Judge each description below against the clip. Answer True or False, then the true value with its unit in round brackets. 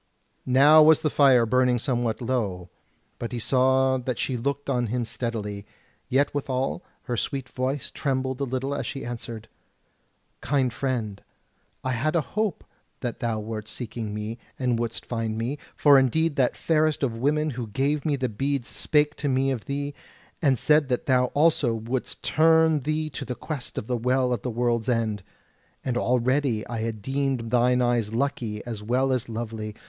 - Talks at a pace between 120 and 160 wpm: False (175 wpm)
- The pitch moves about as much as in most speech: True (3.2 semitones)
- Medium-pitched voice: False (125 Hz)